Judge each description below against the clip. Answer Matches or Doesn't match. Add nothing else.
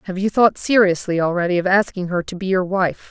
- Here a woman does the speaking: Matches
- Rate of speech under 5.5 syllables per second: Doesn't match